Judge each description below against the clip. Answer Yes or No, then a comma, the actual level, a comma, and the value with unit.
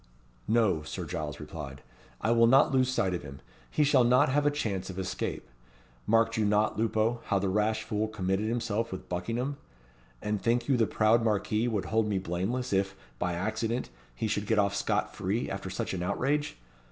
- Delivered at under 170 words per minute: No, average, 190 wpm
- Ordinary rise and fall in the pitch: Yes, average, 3.6 semitones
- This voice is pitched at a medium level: No, low, 110 Hz